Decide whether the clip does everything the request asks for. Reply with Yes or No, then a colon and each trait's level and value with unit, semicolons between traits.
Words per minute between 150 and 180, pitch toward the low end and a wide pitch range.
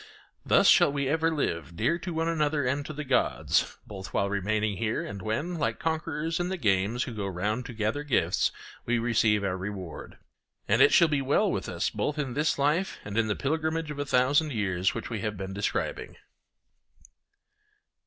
No: average, 190 wpm; low, 125 Hz; wide, 6.6 semitones